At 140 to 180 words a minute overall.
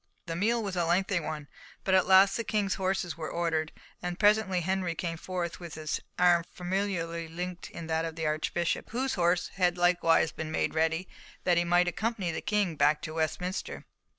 No: average, 190 wpm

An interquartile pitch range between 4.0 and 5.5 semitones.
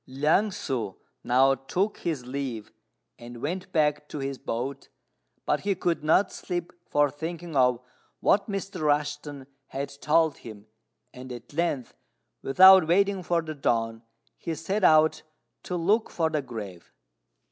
Yes: average, 4.9 semitones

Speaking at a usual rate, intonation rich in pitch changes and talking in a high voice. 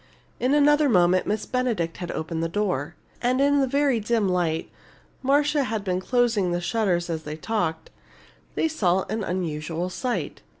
Yes: average, 165 wpm; wide, 6.5 semitones; high, 205 Hz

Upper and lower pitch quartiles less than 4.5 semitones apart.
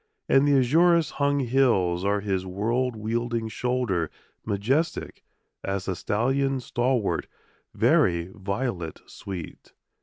No: average, 5.3 semitones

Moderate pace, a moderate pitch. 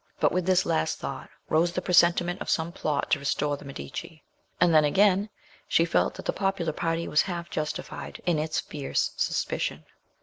Yes: average, 180 wpm; medium, 170 Hz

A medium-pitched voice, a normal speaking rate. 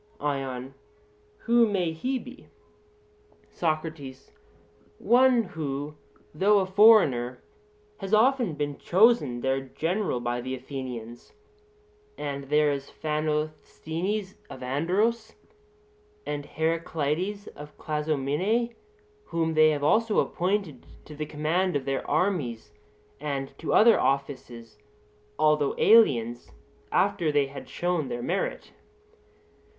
No: medium, 155 Hz; slow, 105 wpm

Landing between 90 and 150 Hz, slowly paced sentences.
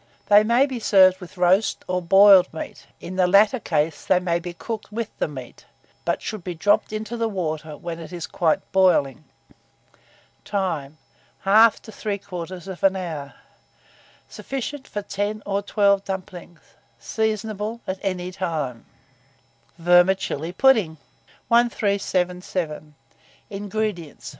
No: high, 190 Hz; slow, 125 wpm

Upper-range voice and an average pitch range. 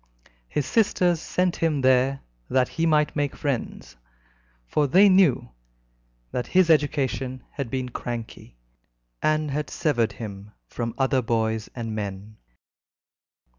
No: low, 130 Hz; average, 4.9 semitones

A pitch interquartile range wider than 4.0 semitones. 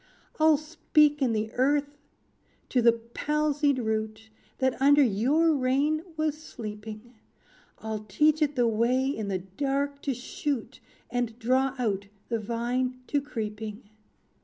Yes: average, 4.6 semitones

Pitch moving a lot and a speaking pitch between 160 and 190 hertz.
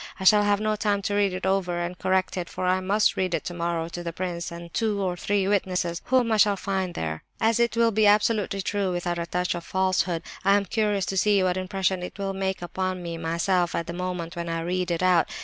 No: narrow, 2.5 semitones; medium, 185 Hz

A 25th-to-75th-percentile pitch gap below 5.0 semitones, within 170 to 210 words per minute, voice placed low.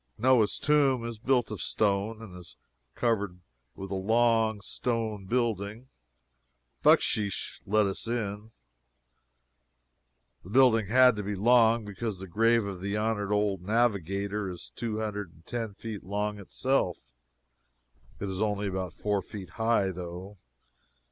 No: average, 2.7 semitones; slow, 135 wpm; low, 105 Hz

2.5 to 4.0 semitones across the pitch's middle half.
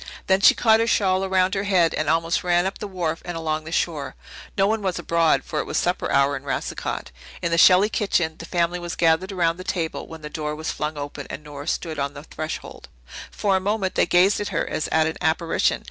Yes: average, 3.2 semitones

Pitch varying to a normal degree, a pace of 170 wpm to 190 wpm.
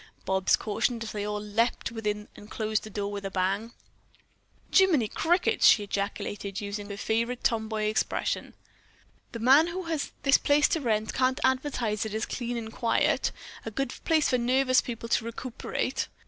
Yes: average, 3.5 semitones; average, 175 wpm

